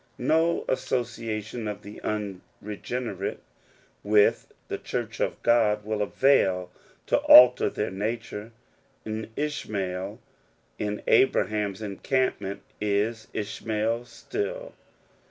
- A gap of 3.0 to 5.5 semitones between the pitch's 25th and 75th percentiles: No, narrow, 2.6 semitones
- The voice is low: Yes, low, 110 Hz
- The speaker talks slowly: Yes, slow, 100 wpm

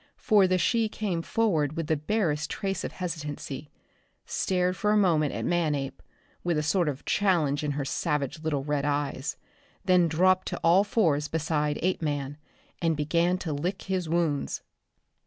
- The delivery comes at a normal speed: Yes, average, 160 wpm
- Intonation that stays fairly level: No, average, 3.8 semitones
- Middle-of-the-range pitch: Yes, medium, 160 Hz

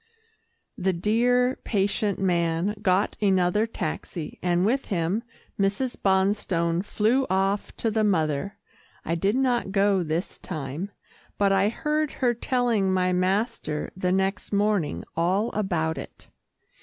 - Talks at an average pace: No, slow, 130 wpm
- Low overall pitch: No, high, 195 Hz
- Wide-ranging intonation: No, average, 3.2 semitones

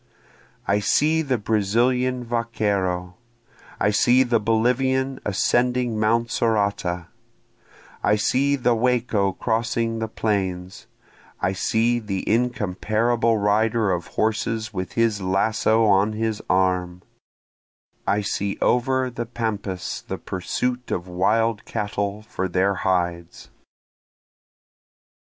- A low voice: Yes, low, 110 Hz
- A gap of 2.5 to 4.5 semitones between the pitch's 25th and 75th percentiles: Yes, average, 3.4 semitones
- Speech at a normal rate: No, slow, 105 wpm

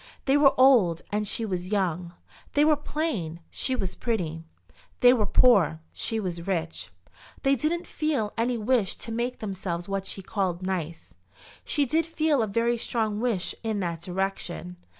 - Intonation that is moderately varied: No, wide, 5.8 semitones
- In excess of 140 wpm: Yes, average, 165 wpm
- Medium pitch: No, high, 210 Hz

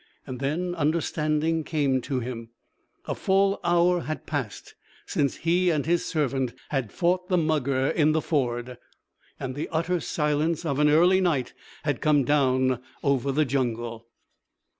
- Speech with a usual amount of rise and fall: Yes, average, 4.1 semitones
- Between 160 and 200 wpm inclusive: No, average, 145 wpm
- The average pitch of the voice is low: No, medium, 150 Hz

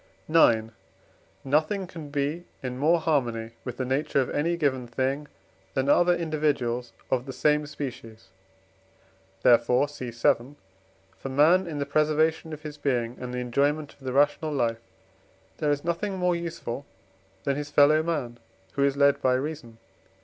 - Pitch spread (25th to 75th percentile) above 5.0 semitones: No, average, 3.6 semitones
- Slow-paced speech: No, average, 155 wpm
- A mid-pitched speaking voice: Yes, medium, 145 Hz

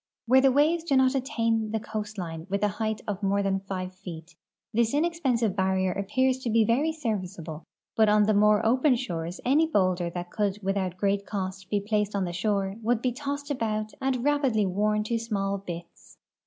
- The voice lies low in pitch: No, high, 210 Hz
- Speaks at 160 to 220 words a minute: Yes, average, 190 wpm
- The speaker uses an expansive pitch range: No, average, 4.3 semitones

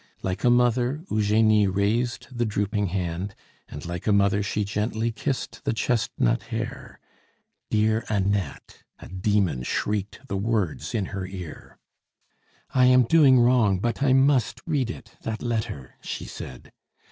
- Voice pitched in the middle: No, low, 105 Hz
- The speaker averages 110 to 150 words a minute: Yes, average, 145 wpm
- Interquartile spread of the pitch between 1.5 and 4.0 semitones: Yes, average, 3.5 semitones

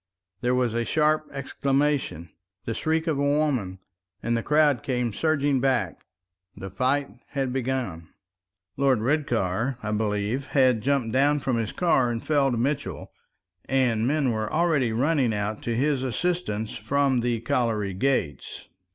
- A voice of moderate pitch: No, low, 130 Hz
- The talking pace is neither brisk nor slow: Yes, average, 145 wpm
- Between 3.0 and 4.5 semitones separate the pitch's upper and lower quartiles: Yes, average, 4.0 semitones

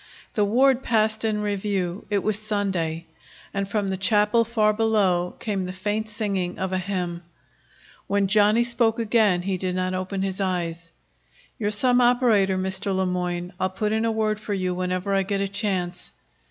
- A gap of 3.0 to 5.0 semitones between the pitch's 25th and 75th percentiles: No, narrow, 2.6 semitones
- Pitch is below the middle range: No, high, 200 Hz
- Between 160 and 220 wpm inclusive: Yes, average, 180 wpm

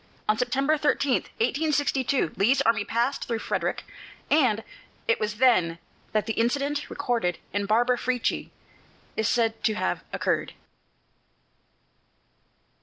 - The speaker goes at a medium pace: No, slow, 115 wpm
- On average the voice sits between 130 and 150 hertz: No, high, 240 Hz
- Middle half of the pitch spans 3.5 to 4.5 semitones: Yes, average, 4.2 semitones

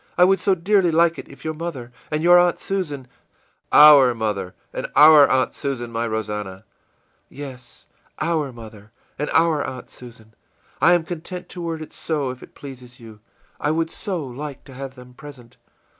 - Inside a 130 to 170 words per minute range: No, average, 180 wpm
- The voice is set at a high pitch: No, medium, 140 Hz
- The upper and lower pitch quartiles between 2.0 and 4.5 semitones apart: No, average, 5.2 semitones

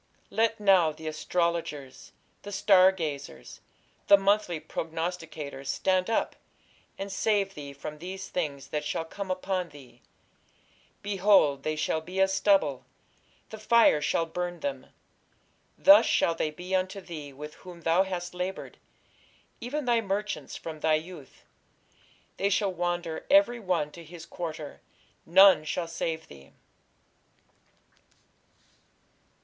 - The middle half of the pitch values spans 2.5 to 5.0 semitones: Yes, average, 4.0 semitones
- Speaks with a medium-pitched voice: Yes, medium, 175 Hz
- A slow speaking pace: Yes, slow, 130 wpm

